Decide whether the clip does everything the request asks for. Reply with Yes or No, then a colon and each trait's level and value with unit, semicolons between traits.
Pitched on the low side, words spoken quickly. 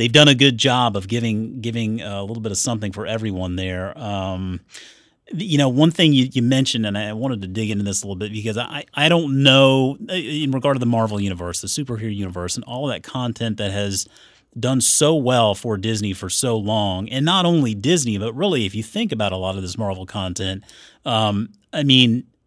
Yes: low, 115 Hz; fast, 215 wpm